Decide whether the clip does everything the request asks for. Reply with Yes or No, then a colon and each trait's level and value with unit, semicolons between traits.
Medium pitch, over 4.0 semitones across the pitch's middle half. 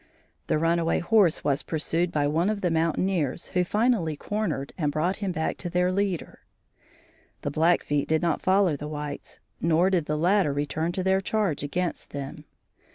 No: medium, 170 Hz; average, 3.6 semitones